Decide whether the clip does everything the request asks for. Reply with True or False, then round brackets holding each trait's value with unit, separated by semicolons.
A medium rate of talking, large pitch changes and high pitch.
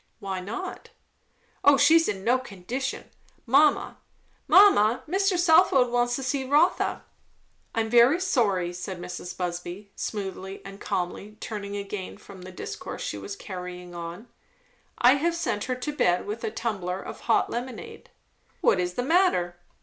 True (150 wpm; 6.6 semitones; 220 Hz)